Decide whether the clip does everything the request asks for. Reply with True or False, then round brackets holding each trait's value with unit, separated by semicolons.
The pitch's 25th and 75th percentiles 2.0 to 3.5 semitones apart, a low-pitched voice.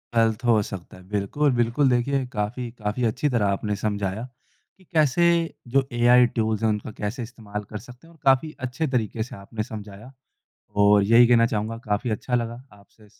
True (3.1 semitones; 115 Hz)